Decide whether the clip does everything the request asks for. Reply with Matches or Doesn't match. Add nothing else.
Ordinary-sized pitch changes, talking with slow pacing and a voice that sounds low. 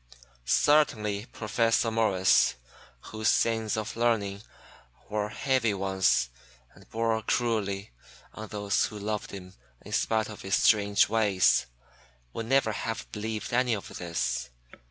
Doesn't match